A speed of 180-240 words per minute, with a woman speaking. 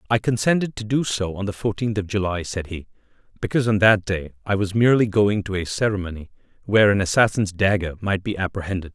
No: average, 200 wpm; male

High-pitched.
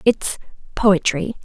Yes: high, 200 Hz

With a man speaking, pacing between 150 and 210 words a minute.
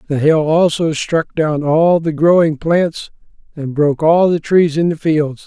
Yes: male; average, 185 wpm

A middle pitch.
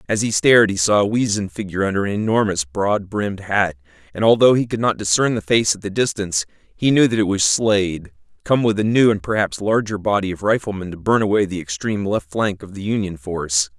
No: low, 100 Hz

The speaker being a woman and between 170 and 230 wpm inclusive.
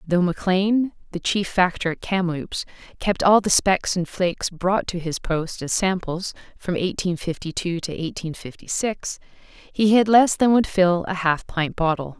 Yes: female; average, 180 wpm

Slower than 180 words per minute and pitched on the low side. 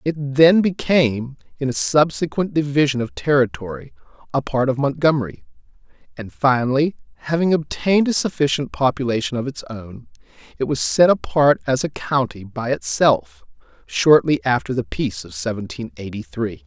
Yes: average, 145 wpm; low, 125 Hz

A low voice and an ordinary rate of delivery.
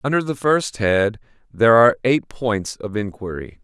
Yes: low, 115 Hz; average, 165 wpm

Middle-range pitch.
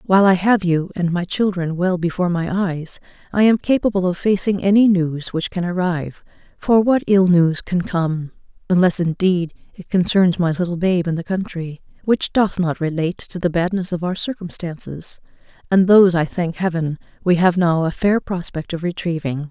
Yes: medium, 180 Hz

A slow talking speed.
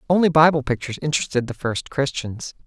No: average, 155 wpm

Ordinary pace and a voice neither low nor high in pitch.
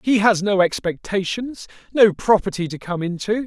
No: average, 155 wpm; high, 200 Hz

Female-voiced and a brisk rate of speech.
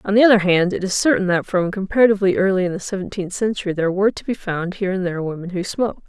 Yes: female; fast, 255 wpm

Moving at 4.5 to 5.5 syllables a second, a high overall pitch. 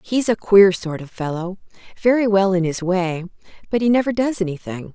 Yes: 5.3 syllables/s; high, 195 Hz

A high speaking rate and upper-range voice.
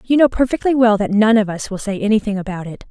Yes: fast, 270 wpm; high, 215 Hz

